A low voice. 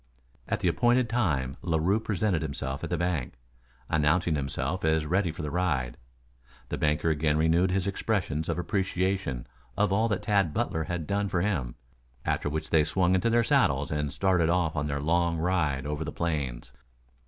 Yes: very low, 85 Hz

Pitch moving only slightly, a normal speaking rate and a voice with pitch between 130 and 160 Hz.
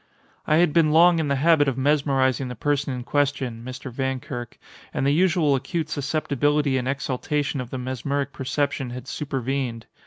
Yes: narrow, 2.2 semitones; average, 165 wpm; medium, 140 Hz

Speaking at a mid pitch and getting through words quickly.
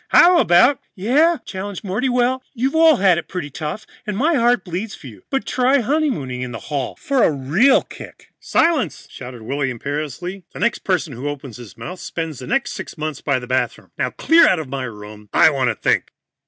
Yes: medium, 175 Hz; fast, 210 wpm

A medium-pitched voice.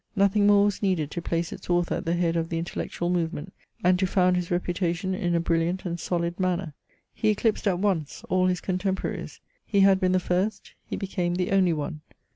Yes: medium, 180 Hz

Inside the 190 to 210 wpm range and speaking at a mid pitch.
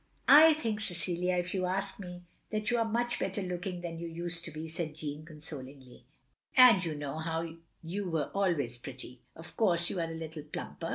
Yes: average, 195 wpm; medium, 175 Hz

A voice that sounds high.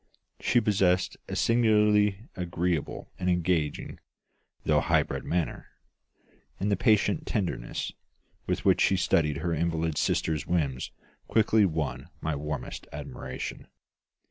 No: very low, 90 Hz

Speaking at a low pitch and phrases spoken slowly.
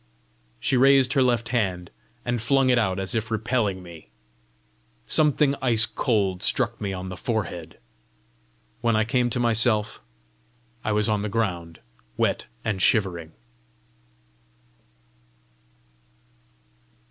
Yes: low, 110 Hz; slow, 120 wpm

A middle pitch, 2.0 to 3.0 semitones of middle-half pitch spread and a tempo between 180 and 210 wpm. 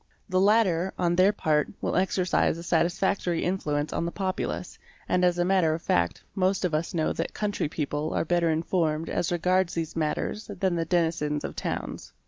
Yes: medium, 175 Hz; narrow, 2.6 semitones; average, 185 wpm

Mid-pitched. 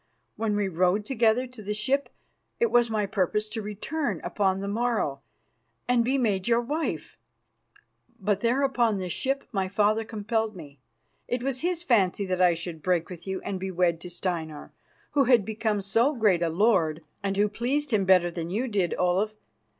No: high, 210 Hz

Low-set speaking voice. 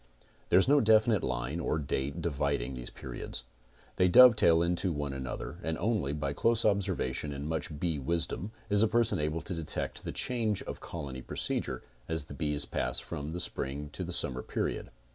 Yes: very low, 80 Hz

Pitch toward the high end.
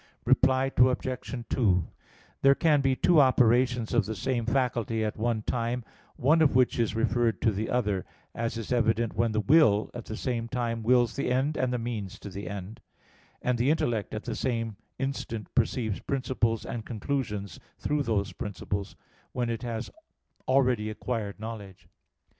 No: low, 115 Hz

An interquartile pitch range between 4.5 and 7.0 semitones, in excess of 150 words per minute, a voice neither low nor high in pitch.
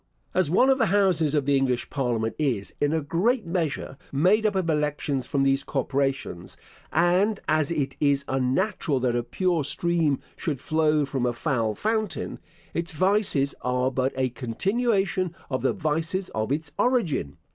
Yes: wide, 5.5 semitones; average, 165 wpm; medium, 150 Hz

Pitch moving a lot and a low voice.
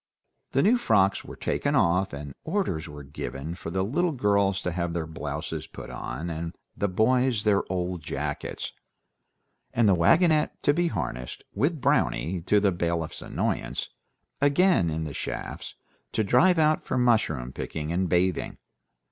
Yes: wide, 7.6 semitones; very low, 95 Hz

